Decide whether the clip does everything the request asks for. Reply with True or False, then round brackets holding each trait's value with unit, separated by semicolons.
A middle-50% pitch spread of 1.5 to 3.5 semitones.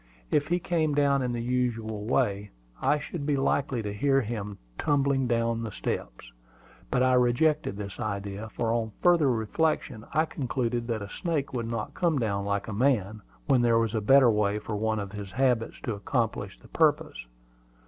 False (4.3 semitones)